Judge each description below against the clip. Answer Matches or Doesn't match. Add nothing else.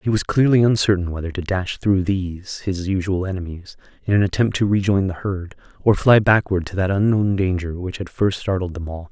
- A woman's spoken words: Doesn't match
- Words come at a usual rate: Doesn't match